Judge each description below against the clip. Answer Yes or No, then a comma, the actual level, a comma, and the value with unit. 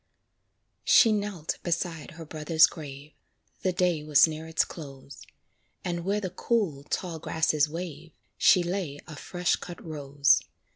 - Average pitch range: Yes, average, 3.0 semitones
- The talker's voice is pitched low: No, medium, 160 Hz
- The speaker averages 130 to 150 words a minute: Yes, average, 140 wpm